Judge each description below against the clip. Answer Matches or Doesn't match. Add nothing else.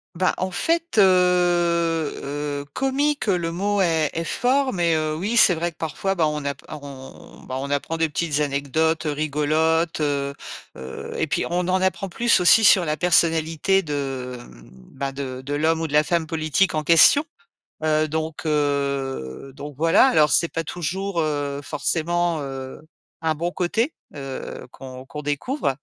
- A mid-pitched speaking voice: Matches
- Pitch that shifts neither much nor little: Matches